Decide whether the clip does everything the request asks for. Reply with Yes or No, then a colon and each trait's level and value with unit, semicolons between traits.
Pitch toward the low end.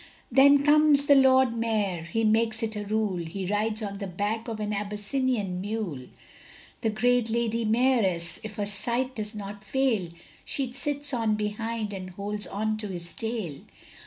No: high, 215 Hz